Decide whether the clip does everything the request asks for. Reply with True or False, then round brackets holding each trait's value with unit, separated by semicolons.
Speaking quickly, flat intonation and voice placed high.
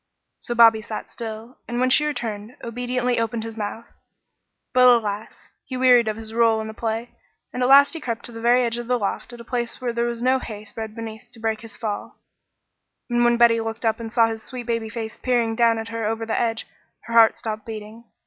True (225 wpm; 1.4 semitones; 230 Hz)